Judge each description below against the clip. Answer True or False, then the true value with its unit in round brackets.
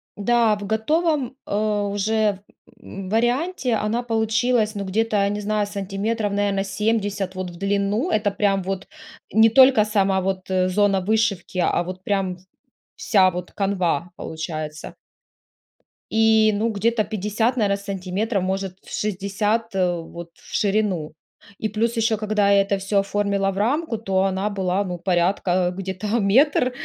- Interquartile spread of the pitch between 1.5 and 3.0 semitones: True (2.4 semitones)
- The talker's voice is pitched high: True (205 Hz)